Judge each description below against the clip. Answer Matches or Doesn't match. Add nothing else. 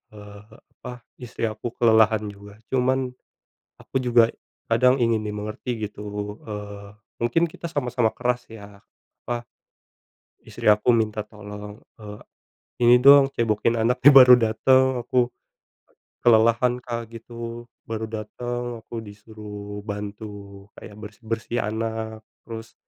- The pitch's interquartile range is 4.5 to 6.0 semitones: Doesn't match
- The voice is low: Matches